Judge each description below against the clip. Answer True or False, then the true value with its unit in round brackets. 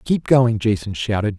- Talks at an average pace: True (175 wpm)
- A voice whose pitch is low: True (110 Hz)